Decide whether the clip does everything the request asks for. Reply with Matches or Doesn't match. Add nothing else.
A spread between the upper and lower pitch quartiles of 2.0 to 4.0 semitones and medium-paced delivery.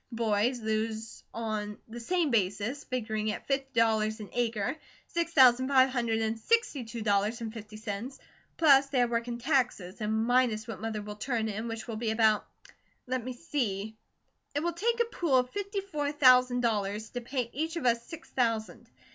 Matches